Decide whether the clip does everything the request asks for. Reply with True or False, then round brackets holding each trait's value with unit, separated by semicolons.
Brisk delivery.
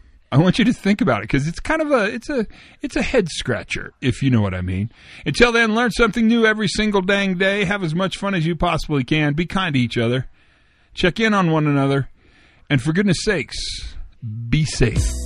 True (225 wpm)